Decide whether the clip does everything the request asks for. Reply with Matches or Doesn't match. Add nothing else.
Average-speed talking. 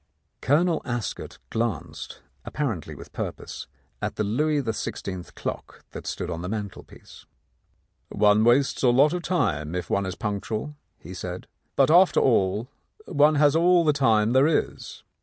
Matches